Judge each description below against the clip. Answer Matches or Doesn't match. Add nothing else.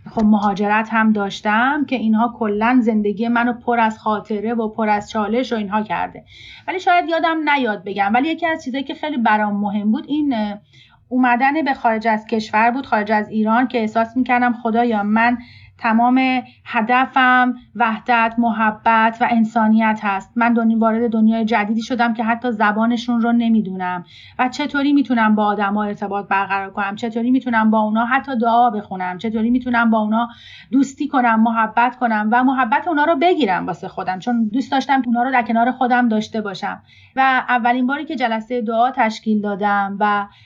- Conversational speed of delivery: Doesn't match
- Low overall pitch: Doesn't match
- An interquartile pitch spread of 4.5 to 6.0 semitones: Doesn't match